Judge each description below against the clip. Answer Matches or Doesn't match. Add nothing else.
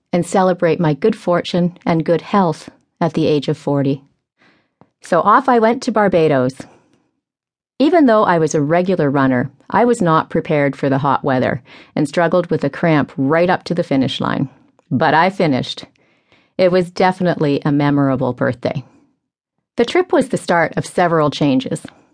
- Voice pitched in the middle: Matches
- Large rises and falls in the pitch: Doesn't match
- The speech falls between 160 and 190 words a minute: Matches